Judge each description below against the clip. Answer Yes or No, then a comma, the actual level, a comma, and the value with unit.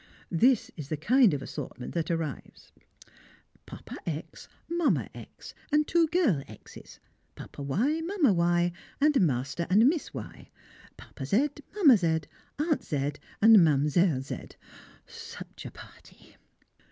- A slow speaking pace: Yes, slow, 130 wpm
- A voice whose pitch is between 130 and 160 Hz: No, medium, 175 Hz